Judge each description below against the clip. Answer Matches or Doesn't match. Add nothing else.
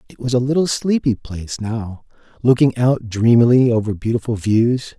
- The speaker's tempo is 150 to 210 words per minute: Matches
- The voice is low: Matches